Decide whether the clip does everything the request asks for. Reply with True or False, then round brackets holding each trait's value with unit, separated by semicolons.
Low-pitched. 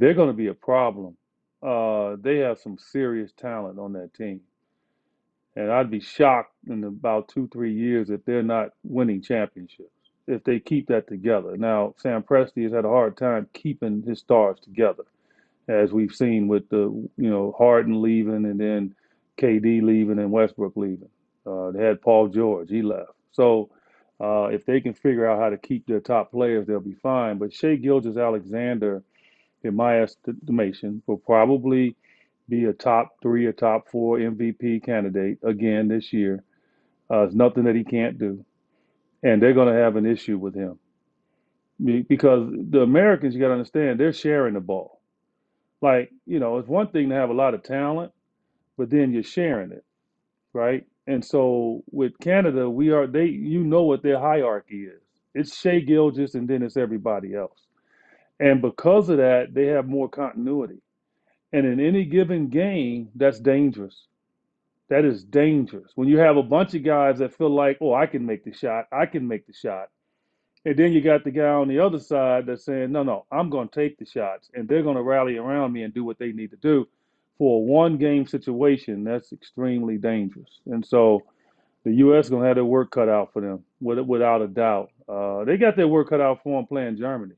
True (120 Hz)